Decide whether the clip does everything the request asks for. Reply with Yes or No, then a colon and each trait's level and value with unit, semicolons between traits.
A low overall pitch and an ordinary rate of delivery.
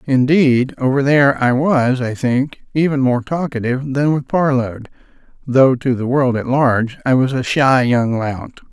Yes: low, 130 Hz; average, 170 wpm